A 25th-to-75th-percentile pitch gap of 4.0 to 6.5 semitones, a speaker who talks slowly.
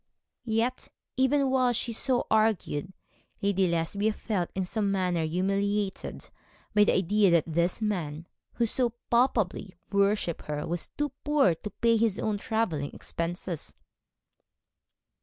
Yes: average, 4.6 semitones; slow, 130 wpm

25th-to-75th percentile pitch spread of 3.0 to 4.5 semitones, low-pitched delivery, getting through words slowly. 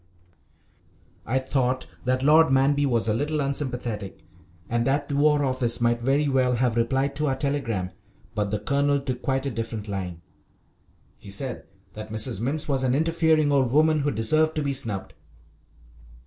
No: average, 3.7 semitones; low, 130 Hz; average, 165 wpm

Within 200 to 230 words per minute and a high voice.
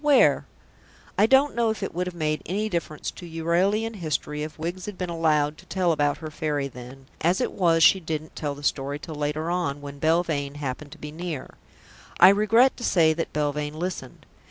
No: fast, 205 wpm; medium, 160 Hz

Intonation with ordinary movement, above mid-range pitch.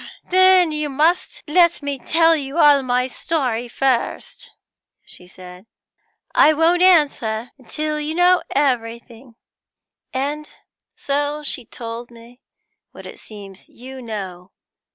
Yes: average, 4.8 semitones; very high, 270 Hz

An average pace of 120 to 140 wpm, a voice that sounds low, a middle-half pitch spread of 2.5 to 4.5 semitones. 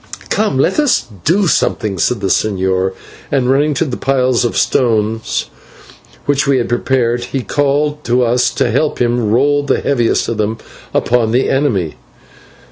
No: average, 160 wpm; low, 125 Hz; average, 3.9 semitones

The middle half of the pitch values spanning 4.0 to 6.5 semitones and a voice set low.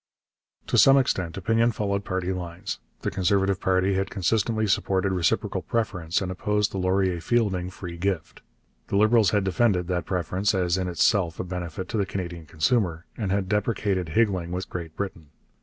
No: narrow, 2.4 semitones; very low, 95 Hz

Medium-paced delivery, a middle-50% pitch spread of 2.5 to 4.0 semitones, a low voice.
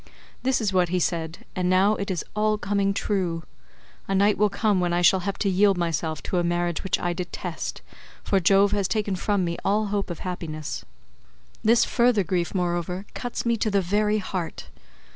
No: average, 195 wpm; average, 2.8 semitones; high, 190 Hz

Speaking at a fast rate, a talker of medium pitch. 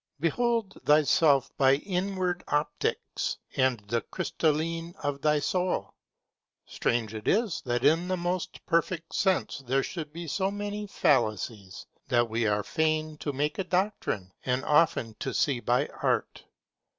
No: average, 140 wpm; medium, 150 Hz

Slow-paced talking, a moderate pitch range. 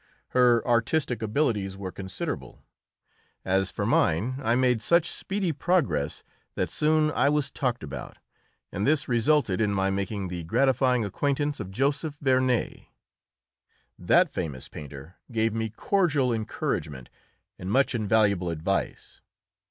No: slow, 130 wpm; wide, 6.4 semitones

